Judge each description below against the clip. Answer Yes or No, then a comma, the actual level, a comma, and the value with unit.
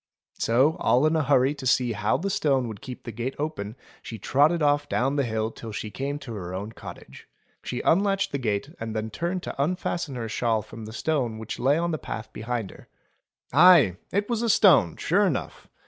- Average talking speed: No, fast, 210 wpm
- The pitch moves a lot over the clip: Yes, wide, 5.9 semitones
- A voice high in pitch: No, low, 130 Hz